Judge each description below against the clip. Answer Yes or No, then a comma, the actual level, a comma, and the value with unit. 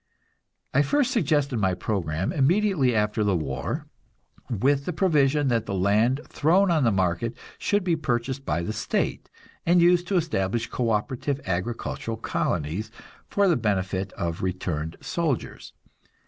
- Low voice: Yes, low, 120 Hz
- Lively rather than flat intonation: Yes, wide, 8.3 semitones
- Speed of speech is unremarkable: Yes, average, 145 wpm